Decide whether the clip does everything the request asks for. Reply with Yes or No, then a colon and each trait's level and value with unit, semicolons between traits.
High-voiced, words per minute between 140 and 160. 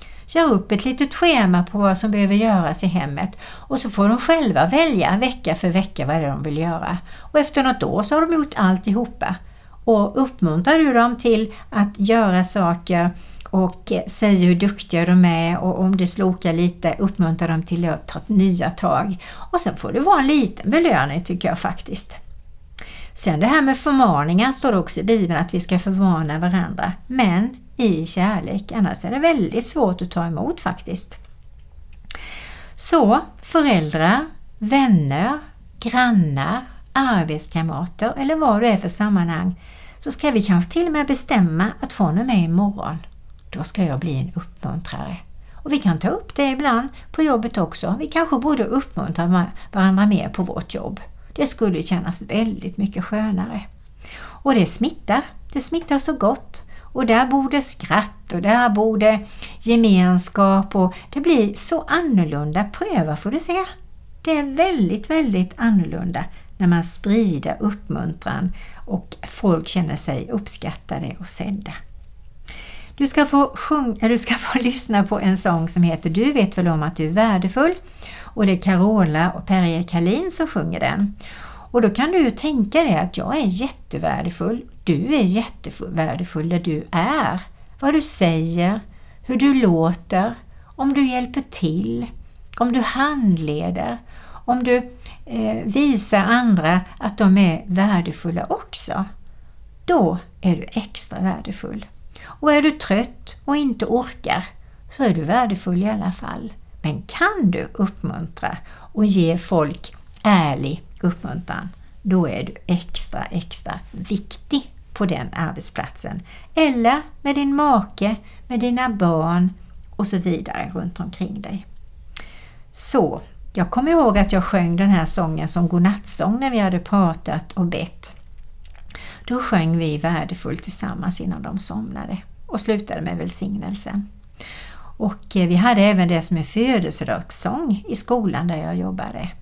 Yes: high, 195 Hz; average, 155 wpm